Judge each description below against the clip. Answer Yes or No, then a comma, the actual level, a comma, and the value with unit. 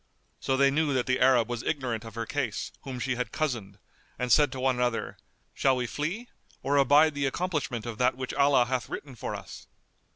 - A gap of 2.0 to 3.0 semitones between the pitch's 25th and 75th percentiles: Yes, average, 2.7 semitones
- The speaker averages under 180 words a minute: No, fast, 205 wpm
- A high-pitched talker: No, low, 130 Hz